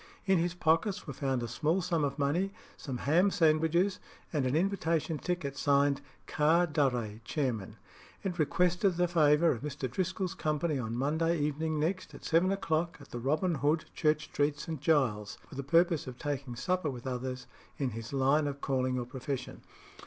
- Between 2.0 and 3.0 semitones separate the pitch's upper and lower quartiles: No, average, 4.1 semitones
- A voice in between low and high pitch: Yes, medium, 150 Hz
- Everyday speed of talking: Yes, average, 175 wpm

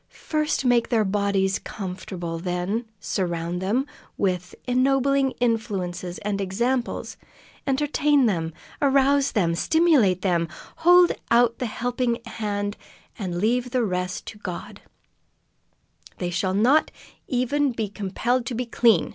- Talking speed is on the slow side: Yes, slow, 120 wpm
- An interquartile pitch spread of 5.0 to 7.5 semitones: Yes, average, 5.3 semitones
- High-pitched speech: Yes, high, 220 Hz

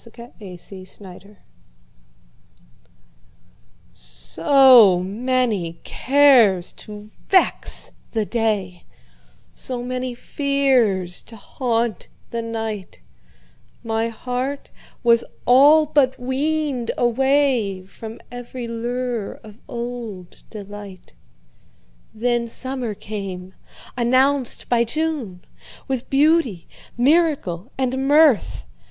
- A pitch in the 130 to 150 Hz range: No, high, 235 Hz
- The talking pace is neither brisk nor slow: No, slow, 75 wpm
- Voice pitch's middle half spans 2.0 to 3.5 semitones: No, average, 4.5 semitones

